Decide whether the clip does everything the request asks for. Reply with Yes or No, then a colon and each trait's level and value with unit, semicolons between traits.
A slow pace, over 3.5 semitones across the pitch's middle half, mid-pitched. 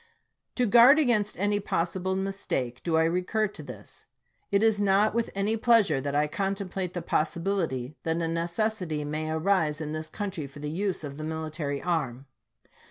No: average, 175 wpm; average, 4.6 semitones; medium, 175 Hz